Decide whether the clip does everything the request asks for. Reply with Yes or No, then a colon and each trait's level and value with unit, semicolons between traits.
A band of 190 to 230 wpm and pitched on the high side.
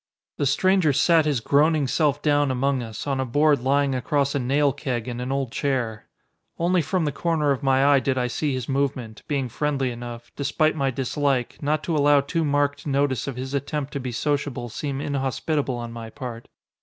No: average, 200 wpm; medium, 140 Hz